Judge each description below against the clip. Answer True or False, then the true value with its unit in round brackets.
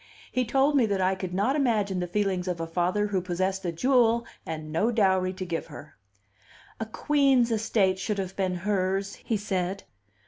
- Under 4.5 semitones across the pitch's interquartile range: True (3.4 semitones)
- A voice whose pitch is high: True (195 Hz)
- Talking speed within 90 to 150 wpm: False (185 wpm)